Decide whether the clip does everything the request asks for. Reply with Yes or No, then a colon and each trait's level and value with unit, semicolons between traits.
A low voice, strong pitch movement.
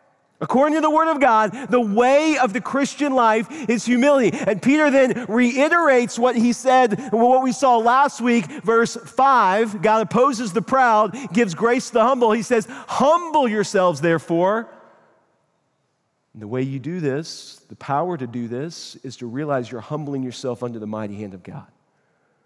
No: high, 230 Hz; wide, 8.0 semitones